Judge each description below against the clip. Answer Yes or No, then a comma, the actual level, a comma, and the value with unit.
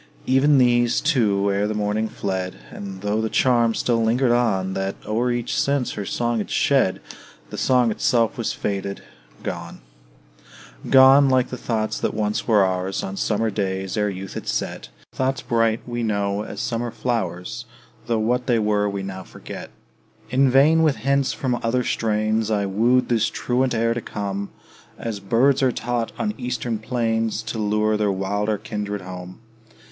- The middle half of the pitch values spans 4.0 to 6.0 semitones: No, average, 3.2 semitones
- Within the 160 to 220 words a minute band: Yes, average, 170 wpm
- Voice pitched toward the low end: Yes, low, 110 Hz